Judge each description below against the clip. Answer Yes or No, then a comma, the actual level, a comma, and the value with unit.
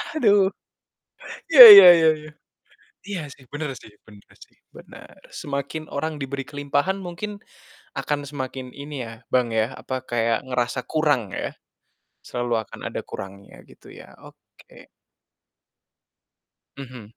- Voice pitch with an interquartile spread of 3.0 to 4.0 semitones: No, average, 4.5 semitones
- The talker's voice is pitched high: No, medium, 140 Hz